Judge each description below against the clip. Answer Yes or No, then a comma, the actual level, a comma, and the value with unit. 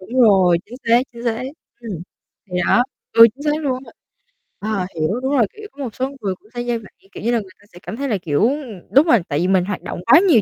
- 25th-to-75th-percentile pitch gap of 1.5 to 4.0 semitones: No, average, 5.1 semitones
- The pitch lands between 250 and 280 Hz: No, high, 230 Hz